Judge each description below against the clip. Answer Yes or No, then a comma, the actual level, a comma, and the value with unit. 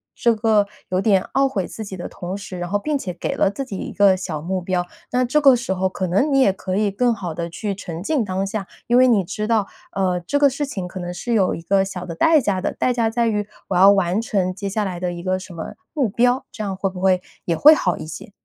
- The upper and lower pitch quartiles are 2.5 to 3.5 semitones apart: No, average, 4.0 semitones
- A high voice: Yes, high, 195 Hz